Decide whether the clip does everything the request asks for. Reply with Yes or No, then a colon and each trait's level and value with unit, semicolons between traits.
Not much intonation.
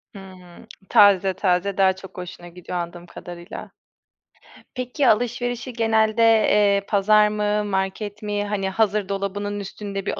Yes: narrow, 2.0 semitones